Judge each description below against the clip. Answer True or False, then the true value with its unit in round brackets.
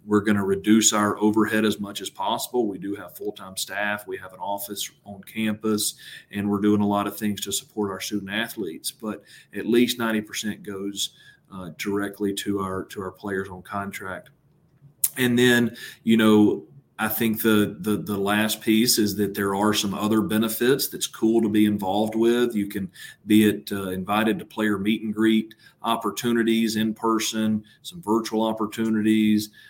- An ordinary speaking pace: True (180 wpm)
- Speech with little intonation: True (1.6 semitones)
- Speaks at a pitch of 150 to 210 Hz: False (105 Hz)